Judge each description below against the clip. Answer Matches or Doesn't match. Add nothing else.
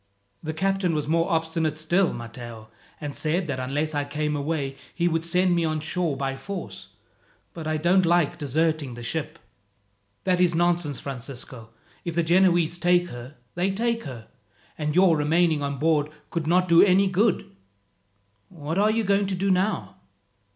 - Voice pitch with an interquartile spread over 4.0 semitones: Doesn't match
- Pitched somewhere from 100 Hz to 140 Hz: Doesn't match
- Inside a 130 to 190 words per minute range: Matches